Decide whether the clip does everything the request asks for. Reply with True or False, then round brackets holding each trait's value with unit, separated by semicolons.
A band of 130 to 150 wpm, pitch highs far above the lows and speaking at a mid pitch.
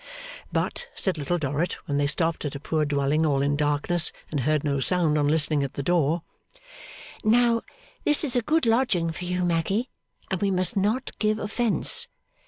False (185 wpm; 6.4 semitones; 170 Hz)